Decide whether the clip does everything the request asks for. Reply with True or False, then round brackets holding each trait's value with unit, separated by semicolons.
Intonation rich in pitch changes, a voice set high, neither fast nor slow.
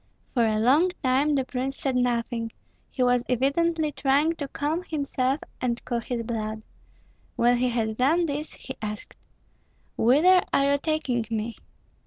False (3.7 semitones; 255 Hz; 155 wpm)